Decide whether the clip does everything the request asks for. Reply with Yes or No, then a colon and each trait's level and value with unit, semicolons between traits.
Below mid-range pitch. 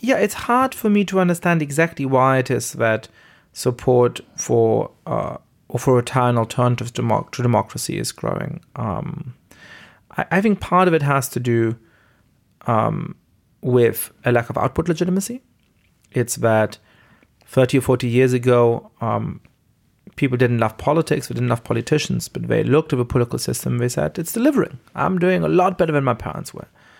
Yes: low, 130 Hz